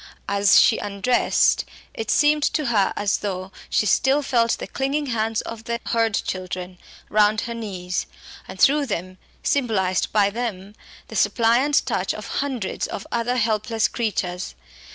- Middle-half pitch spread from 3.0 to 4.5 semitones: Yes, average, 3.5 semitones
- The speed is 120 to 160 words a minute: Yes, average, 150 wpm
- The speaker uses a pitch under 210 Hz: No, high, 220 Hz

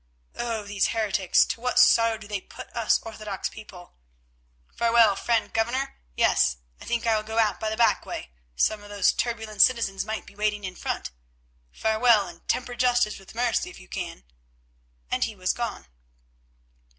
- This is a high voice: Yes, high, 220 Hz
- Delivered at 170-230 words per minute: Yes, average, 175 wpm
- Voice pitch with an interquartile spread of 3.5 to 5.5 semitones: No, narrow, 2.4 semitones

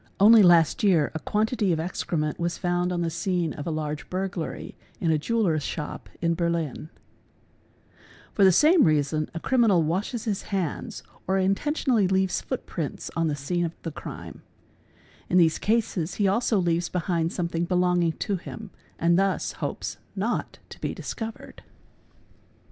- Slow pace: No, average, 160 wpm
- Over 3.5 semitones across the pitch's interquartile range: No, average, 3.2 semitones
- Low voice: No, medium, 175 Hz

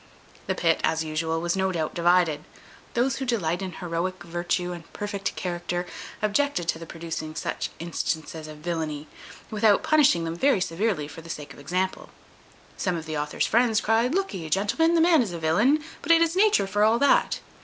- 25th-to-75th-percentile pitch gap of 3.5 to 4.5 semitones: No, wide, 5.4 semitones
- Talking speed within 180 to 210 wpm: Yes, average, 185 wpm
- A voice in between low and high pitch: Yes, medium, 180 Hz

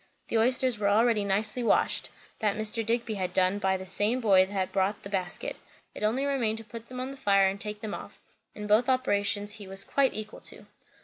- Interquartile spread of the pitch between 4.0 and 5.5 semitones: No, average, 2.7 semitones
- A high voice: Yes, high, 210 Hz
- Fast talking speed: Yes, fast, 225 wpm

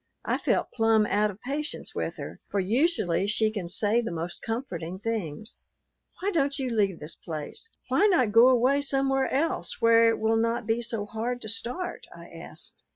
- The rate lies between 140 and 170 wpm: No, average, 185 wpm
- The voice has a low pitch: No, high, 225 Hz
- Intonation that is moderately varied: Yes, average, 4.2 semitones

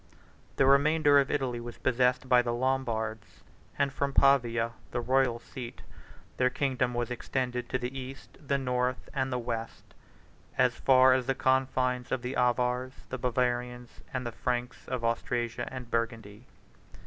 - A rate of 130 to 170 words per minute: Yes, average, 155 wpm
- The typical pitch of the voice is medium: No, low, 125 Hz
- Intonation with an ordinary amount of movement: No, narrow, 1.6 semitones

